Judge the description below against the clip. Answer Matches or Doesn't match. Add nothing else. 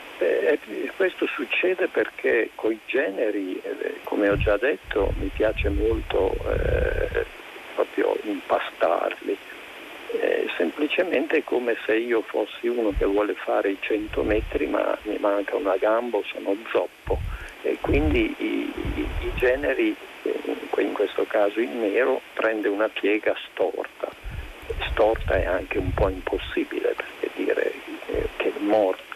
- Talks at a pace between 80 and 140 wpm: Matches